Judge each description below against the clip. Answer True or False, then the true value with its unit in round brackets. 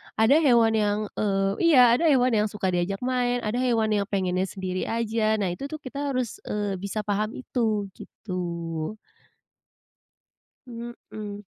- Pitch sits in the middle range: False (215 Hz)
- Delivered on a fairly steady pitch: False (3.5 semitones)